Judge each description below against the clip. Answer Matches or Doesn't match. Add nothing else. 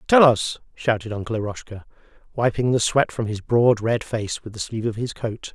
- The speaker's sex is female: Doesn't match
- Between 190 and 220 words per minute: Matches